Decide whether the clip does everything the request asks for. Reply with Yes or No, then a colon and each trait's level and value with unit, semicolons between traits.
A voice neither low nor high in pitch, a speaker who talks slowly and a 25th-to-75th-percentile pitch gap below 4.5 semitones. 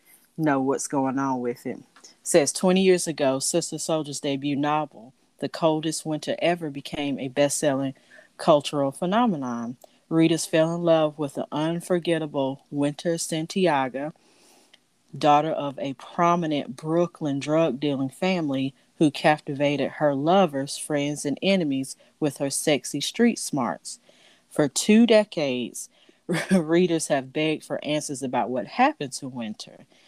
Yes: medium, 150 Hz; slow, 130 wpm; average, 3.1 semitones